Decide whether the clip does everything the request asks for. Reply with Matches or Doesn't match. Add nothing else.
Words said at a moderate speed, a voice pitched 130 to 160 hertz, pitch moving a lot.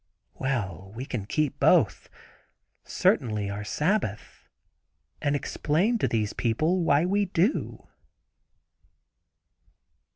Doesn't match